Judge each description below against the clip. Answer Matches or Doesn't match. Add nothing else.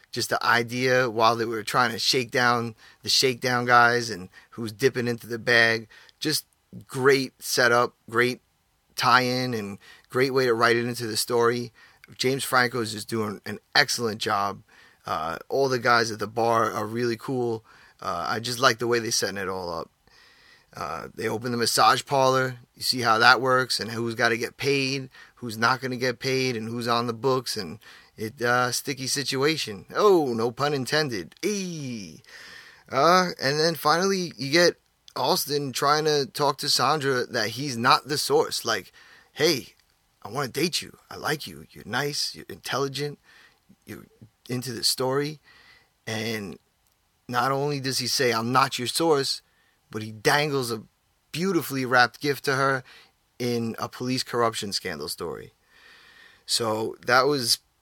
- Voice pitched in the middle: Doesn't match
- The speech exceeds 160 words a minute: Matches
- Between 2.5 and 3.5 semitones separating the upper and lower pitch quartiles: Matches